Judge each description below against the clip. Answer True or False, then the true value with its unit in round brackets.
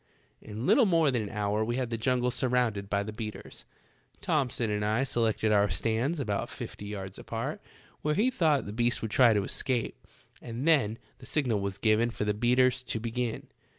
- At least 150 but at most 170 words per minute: False (195 wpm)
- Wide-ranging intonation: False (3.3 semitones)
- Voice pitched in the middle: False (115 Hz)